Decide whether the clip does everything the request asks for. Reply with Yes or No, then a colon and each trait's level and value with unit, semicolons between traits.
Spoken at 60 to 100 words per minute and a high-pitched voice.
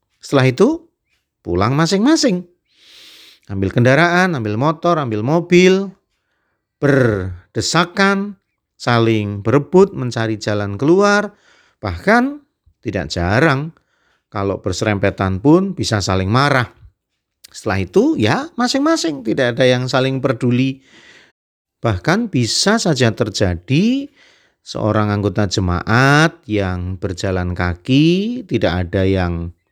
No: average, 95 wpm; low, 130 Hz